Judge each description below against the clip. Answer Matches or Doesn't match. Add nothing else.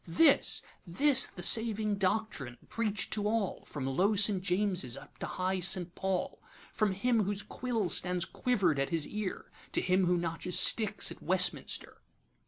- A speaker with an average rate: Matches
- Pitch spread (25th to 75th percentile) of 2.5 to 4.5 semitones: Matches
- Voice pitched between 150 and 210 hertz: Matches